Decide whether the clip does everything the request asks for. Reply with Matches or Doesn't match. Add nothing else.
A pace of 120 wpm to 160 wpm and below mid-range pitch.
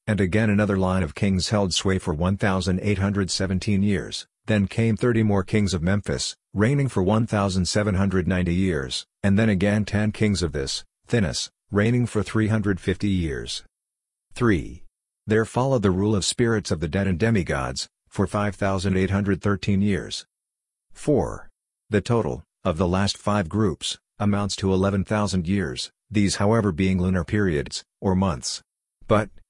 Matches